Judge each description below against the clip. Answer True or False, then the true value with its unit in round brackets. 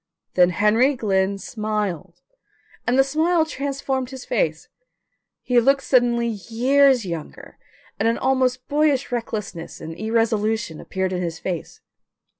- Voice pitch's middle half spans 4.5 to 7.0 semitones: True (5.4 semitones)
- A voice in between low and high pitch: False (230 Hz)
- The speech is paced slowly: True (125 wpm)